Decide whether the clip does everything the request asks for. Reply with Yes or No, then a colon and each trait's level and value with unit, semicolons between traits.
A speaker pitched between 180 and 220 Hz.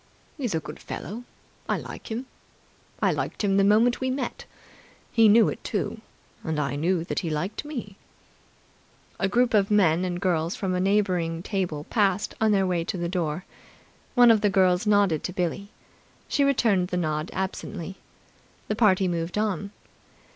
Yes: high, 190 Hz